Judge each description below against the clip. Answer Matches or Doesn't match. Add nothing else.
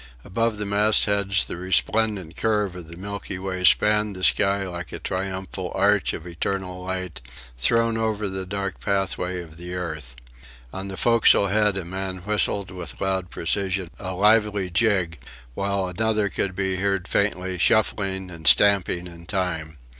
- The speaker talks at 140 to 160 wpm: Matches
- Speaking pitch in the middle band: Doesn't match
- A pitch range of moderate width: Doesn't match